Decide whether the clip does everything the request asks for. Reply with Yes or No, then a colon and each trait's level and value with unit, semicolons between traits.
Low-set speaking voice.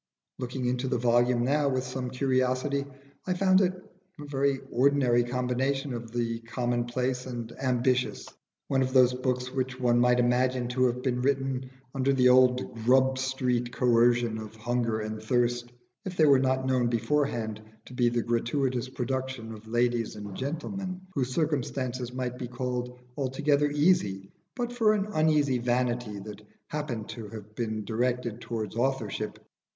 Yes: low, 125 Hz